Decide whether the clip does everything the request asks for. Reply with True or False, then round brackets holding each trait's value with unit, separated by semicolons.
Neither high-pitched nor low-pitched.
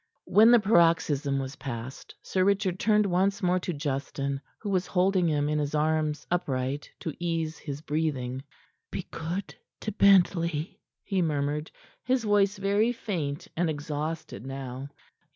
True (160 Hz)